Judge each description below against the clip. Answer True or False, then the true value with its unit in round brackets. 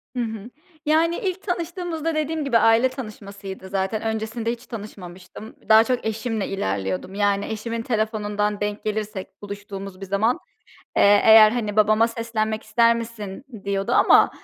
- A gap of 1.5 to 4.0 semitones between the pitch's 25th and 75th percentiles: True (2.6 semitones)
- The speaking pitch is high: True (220 Hz)